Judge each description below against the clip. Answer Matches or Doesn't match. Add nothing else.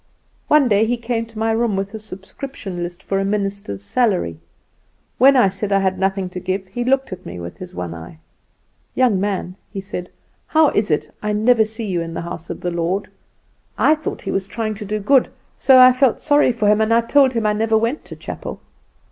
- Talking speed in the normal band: Doesn't match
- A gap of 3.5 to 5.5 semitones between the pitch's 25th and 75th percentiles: Matches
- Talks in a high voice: Matches